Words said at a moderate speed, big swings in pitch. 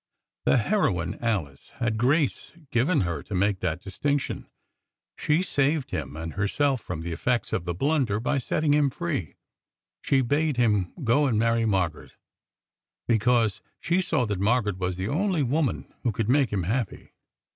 Yes: average, 160 wpm; wide, 6.8 semitones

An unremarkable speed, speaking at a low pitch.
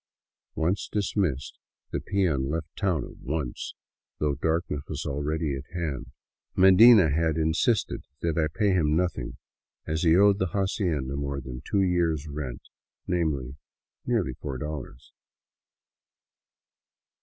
No: slow, 130 wpm; very low, 80 Hz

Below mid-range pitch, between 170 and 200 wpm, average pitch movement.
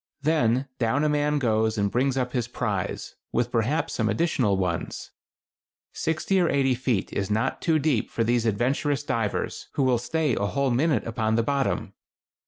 Yes: low, 125 Hz; average, 175 wpm; average, 4.2 semitones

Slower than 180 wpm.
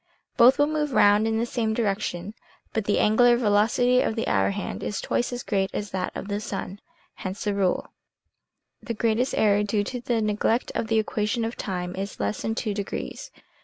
No: average, 195 wpm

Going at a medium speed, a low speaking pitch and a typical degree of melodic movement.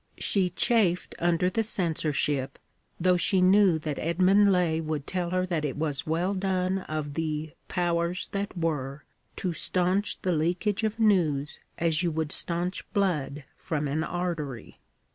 No: average, 150 wpm; medium, 170 Hz; average, 3.1 semitones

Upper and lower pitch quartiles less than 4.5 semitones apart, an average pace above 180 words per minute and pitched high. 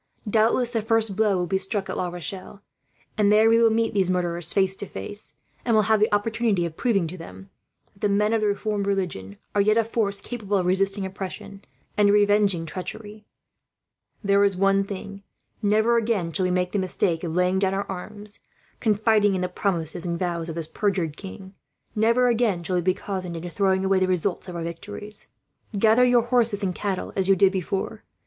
Yes: average, 2.7 semitones; fast, 205 wpm; high, 200 Hz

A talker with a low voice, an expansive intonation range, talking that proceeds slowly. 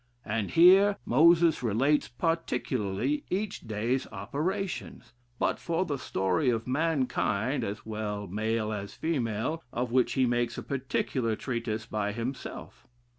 Yes: low, 125 Hz; wide, 6.2 semitones; slow, 125 wpm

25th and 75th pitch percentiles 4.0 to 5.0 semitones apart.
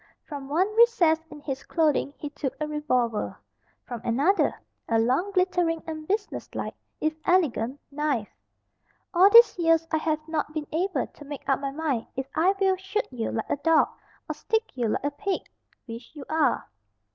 Yes: average, 4.4 semitones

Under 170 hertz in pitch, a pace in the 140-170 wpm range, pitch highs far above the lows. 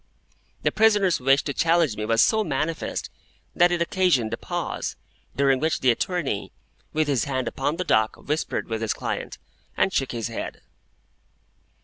Yes: medium, 140 Hz; average, 160 wpm; wide, 5.8 semitones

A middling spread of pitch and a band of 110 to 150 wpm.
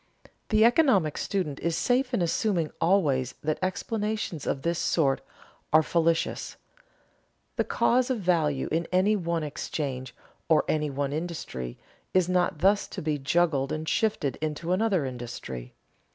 Yes: average, 4.6 semitones; average, 140 wpm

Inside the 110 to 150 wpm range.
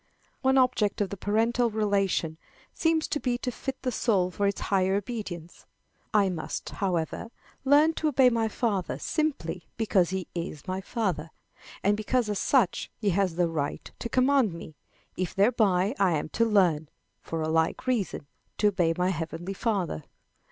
No: average, 165 wpm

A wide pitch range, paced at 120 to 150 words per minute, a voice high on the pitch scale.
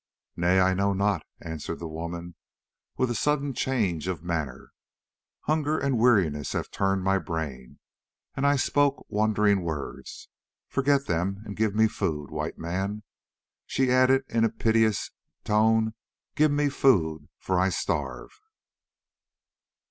No: wide, 6.7 semitones; slow, 135 wpm; low, 100 Hz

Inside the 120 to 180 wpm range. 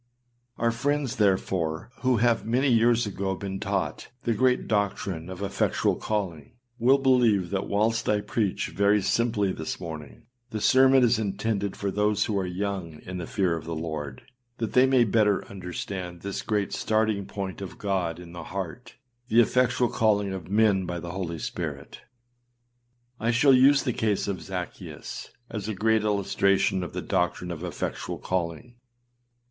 Yes: average, 165 wpm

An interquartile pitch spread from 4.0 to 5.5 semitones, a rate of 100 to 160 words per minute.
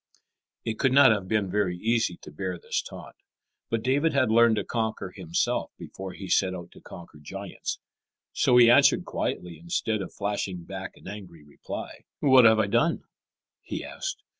No: average, 4.4 semitones; average, 175 wpm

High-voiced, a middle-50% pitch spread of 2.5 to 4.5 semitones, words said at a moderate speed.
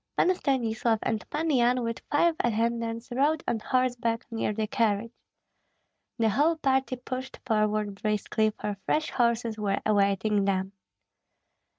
No: high, 230 Hz; average, 3.2 semitones; slow, 130 wpm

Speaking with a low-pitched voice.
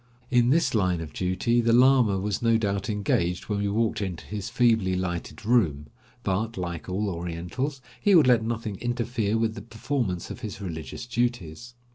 Yes: low, 105 Hz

